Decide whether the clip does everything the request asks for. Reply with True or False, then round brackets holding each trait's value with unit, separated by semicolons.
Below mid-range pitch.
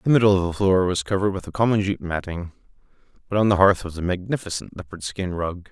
True (95 Hz)